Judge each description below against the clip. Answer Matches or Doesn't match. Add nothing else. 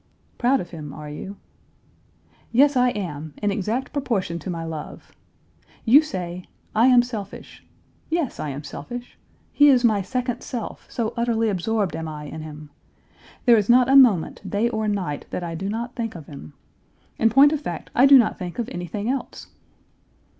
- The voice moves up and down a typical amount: Doesn't match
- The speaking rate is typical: Matches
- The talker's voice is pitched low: Doesn't match